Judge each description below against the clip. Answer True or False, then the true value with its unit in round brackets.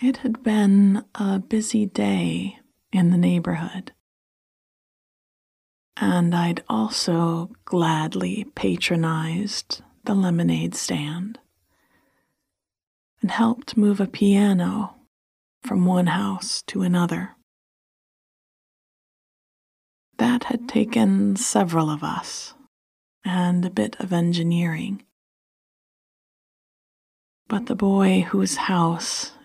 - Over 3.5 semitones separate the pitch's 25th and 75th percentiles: True (3.9 semitones)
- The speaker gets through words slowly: True (90 wpm)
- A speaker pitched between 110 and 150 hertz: False (190 Hz)